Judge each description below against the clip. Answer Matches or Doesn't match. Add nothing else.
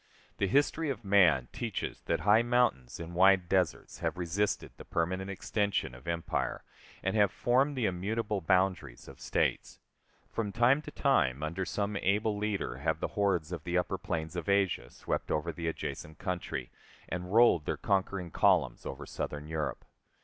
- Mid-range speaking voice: Doesn't match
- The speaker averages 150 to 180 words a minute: Matches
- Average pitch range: Matches